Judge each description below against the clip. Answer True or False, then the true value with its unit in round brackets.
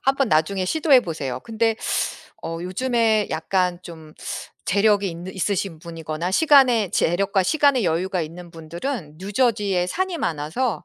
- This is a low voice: False (190 Hz)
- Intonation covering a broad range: True (5.7 semitones)